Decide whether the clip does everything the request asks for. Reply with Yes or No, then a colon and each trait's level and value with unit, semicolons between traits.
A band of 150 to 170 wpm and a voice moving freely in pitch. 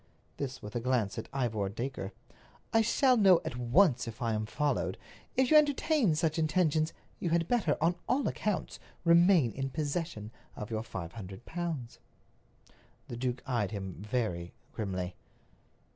Yes: average, 155 wpm; wide, 7.7 semitones